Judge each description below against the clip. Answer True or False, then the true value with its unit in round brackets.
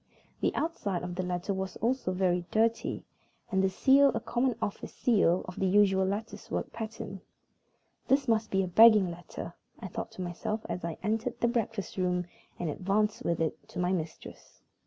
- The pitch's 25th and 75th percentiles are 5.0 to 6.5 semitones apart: False (3.8 semitones)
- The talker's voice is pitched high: True (195 Hz)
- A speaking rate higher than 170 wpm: True (180 wpm)